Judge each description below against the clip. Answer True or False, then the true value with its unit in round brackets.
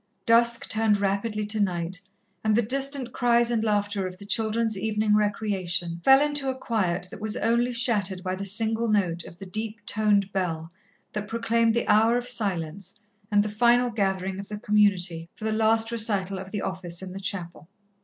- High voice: True (210 Hz)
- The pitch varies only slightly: False (3.2 semitones)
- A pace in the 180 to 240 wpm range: True (185 wpm)